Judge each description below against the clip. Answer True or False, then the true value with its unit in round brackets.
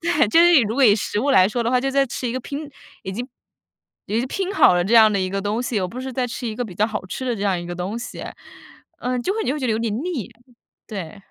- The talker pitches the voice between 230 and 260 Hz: True (235 Hz)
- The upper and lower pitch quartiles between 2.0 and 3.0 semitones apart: False (4.4 semitones)